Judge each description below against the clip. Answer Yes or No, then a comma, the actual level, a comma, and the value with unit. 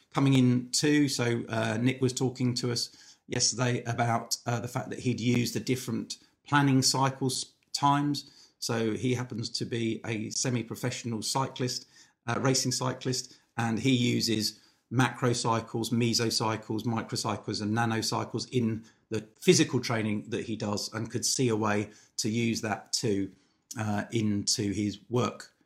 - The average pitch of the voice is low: Yes, low, 120 Hz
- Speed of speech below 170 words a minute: Yes, average, 150 wpm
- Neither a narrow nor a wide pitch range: No, narrow, 2.3 semitones